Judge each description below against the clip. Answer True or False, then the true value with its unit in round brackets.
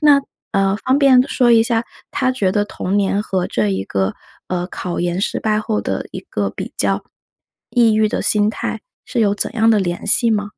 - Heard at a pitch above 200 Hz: True (210 Hz)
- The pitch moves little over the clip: False (3.5 semitones)